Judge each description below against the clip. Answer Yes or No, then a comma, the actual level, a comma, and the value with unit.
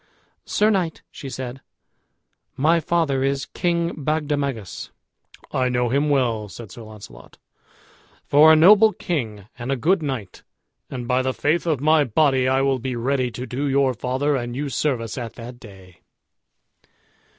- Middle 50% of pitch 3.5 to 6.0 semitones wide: Yes, average, 3.9 semitones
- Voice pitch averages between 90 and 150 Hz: Yes, low, 135 Hz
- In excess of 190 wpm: No, average, 155 wpm